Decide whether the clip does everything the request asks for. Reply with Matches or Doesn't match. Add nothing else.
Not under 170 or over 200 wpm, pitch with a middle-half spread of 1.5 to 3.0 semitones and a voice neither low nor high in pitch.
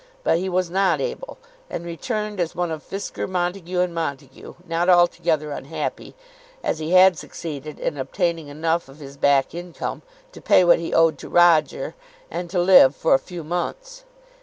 Matches